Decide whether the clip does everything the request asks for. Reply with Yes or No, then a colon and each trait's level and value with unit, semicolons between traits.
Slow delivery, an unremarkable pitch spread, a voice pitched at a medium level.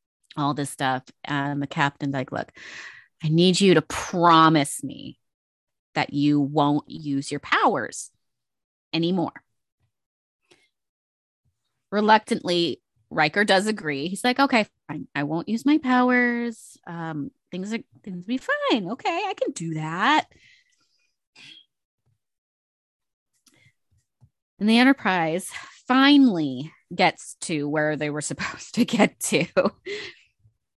No: slow, 115 wpm; wide, 7.9 semitones; medium, 165 Hz